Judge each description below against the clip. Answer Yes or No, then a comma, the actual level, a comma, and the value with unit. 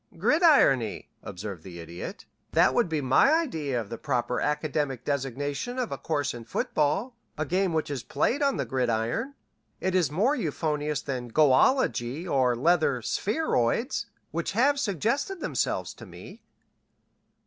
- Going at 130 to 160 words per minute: Yes, average, 145 wpm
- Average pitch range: No, wide, 8.7 semitones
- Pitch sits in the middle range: Yes, medium, 150 Hz